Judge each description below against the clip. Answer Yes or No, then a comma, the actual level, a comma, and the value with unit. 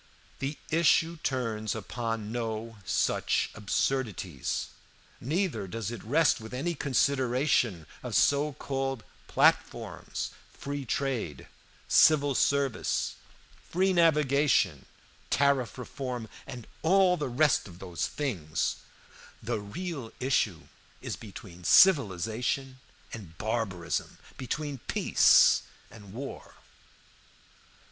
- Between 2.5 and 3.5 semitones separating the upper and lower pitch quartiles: No, average, 4.8 semitones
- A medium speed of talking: No, slow, 95 wpm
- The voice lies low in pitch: Yes, low, 125 Hz